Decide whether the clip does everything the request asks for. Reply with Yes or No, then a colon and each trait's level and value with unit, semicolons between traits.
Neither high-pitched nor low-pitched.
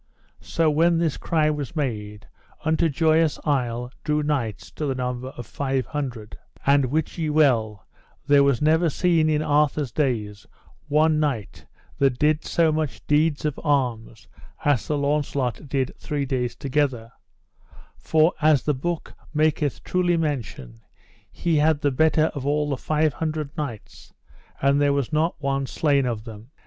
Yes: medium, 145 Hz